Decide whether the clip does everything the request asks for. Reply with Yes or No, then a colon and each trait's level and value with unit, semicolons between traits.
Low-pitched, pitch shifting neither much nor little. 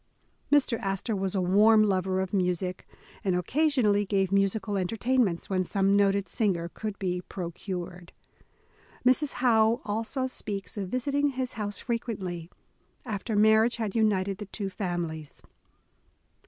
No: high, 200 Hz; average, 3.3 semitones